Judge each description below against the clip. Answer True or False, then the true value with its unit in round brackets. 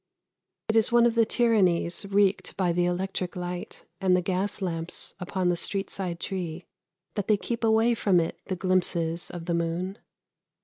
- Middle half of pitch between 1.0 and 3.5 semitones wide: True (2.6 semitones)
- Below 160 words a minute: False (175 wpm)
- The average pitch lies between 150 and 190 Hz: True (185 Hz)